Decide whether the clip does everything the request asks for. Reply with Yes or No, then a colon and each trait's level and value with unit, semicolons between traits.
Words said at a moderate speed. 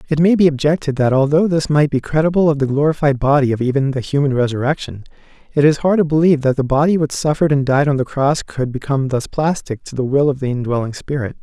No: fast, 235 wpm